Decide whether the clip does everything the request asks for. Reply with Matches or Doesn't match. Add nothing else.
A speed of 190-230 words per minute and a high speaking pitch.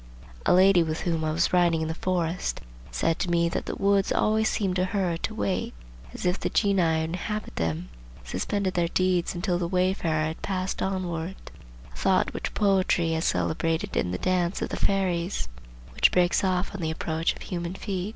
Doesn't match